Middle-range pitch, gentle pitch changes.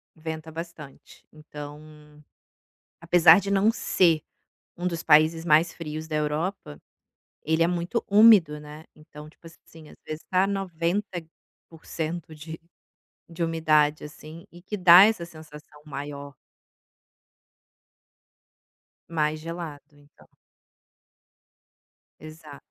Yes: medium, 160 Hz; narrow, 2.2 semitones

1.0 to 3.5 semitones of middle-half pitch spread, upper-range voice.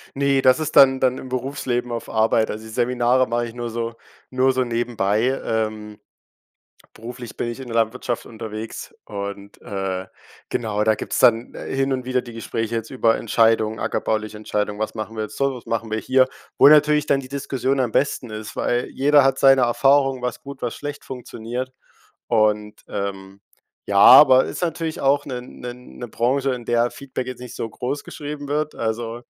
No: average, 3.1 semitones; low, 120 Hz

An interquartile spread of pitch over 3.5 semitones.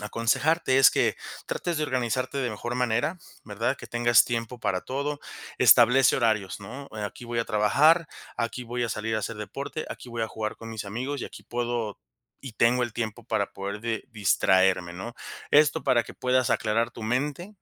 No: average, 3.0 semitones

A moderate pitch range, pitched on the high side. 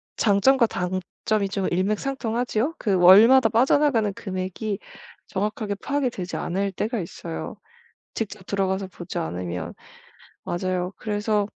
Yes: average, 3.3 semitones; high, 200 Hz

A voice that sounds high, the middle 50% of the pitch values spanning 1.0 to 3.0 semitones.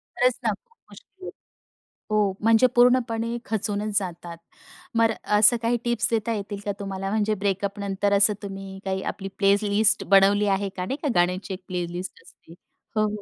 Yes: high, 205 Hz; narrow, 2.5 semitones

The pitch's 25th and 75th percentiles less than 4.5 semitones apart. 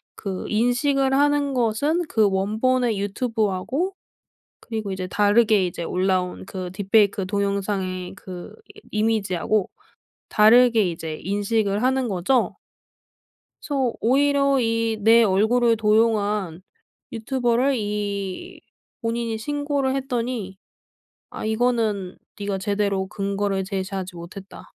Yes: average, 3.9 semitones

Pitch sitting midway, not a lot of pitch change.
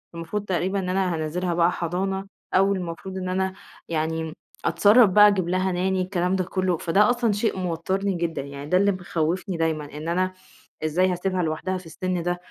Yes: medium, 180 Hz; narrow, 2.3 semitones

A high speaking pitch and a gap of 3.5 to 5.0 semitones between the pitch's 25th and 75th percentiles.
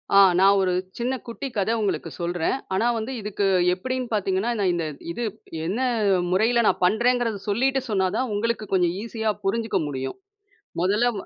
Yes: high, 210 Hz; average, 4.0 semitones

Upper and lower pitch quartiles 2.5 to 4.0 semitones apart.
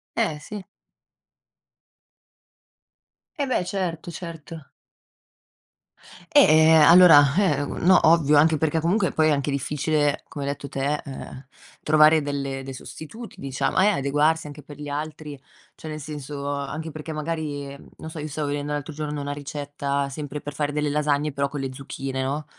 No: narrow, 1.9 semitones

